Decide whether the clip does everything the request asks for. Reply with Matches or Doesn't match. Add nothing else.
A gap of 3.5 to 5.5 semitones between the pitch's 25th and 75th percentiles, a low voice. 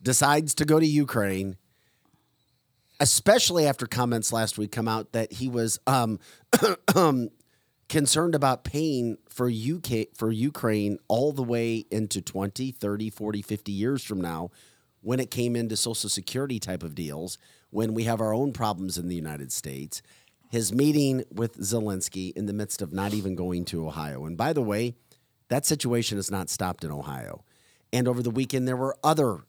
Matches